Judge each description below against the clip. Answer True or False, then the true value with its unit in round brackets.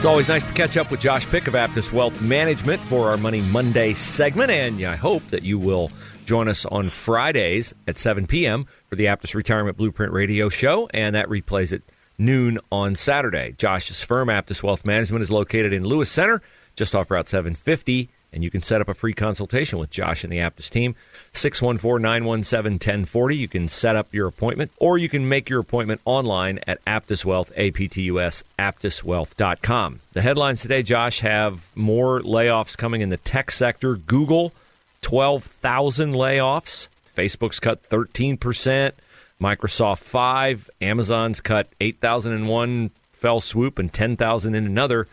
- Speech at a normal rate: True (165 wpm)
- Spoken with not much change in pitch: False (3.8 semitones)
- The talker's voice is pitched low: True (110 Hz)